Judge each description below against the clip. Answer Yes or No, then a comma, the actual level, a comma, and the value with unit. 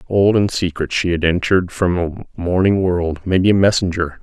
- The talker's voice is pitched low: Yes, very low, 90 Hz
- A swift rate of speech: No, average, 185 wpm